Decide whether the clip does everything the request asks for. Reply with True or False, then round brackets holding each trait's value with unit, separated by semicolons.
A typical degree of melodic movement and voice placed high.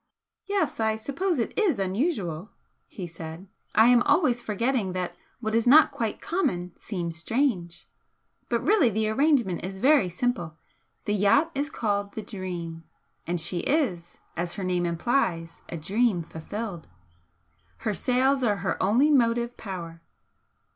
False (6.0 semitones; 210 Hz)